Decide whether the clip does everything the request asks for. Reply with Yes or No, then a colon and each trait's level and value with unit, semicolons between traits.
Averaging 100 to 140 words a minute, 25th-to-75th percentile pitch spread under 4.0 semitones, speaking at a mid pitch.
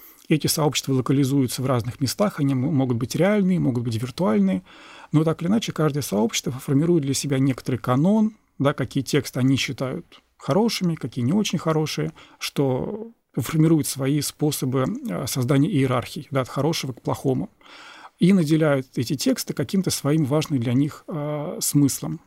No: average, 150 wpm; average, 3.6 semitones; medium, 145 Hz